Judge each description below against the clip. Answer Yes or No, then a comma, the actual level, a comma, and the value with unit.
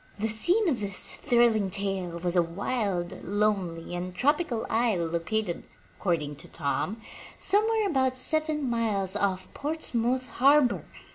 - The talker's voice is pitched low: No, high, 215 Hz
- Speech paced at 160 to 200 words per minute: No, slow, 135 wpm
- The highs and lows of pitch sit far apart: Yes, wide, 6.1 semitones